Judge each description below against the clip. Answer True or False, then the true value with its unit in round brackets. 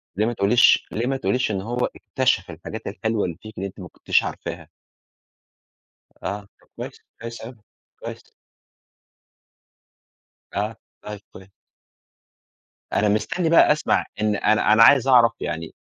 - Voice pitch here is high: False (110 Hz)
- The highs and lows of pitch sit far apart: False (3.5 semitones)